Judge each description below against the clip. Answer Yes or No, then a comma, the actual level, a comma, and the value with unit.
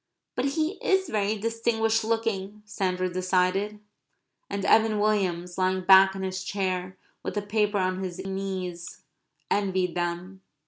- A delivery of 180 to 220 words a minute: No, slow, 135 wpm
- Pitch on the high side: Yes, high, 195 Hz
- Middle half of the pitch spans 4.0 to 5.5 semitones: No, narrow, 2.5 semitones